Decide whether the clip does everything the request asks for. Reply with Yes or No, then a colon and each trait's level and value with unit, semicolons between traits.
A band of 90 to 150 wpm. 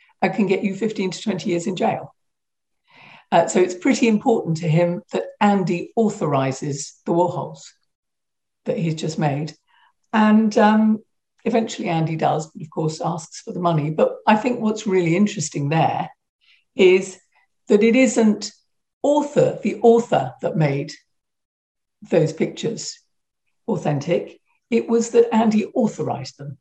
Yes: average, 140 wpm